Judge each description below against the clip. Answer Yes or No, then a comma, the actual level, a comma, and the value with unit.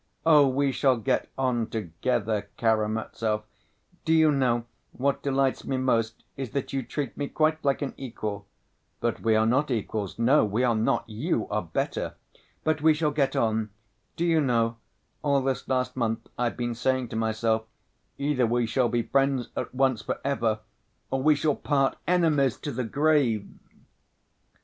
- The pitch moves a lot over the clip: No, average, 3.7 semitones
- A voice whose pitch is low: Yes, low, 125 Hz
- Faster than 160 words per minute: Yes, average, 170 wpm